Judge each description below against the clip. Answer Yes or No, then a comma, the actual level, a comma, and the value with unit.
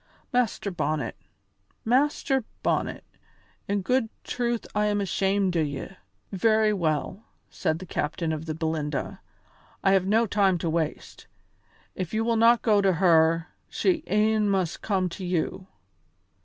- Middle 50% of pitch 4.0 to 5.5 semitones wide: Yes, average, 4.7 semitones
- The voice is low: No, high, 195 Hz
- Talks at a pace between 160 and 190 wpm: No, average, 140 wpm